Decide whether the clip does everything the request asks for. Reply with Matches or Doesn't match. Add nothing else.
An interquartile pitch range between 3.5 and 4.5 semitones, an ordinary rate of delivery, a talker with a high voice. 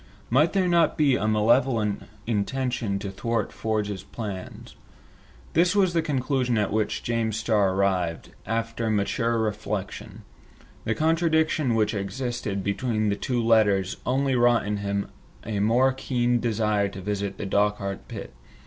Doesn't match